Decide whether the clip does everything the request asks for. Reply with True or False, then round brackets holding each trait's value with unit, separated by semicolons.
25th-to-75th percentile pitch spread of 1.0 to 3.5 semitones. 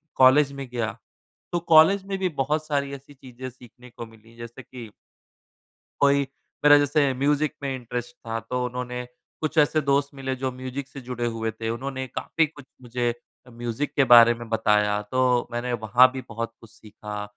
True (3.1 semitones)